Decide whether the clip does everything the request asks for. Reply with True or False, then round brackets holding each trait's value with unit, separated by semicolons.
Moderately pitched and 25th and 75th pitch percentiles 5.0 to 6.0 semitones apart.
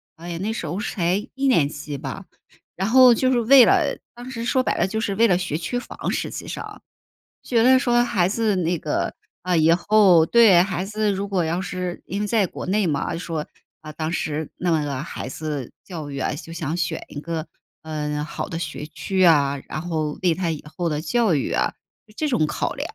True (175 Hz; 5.4 semitones)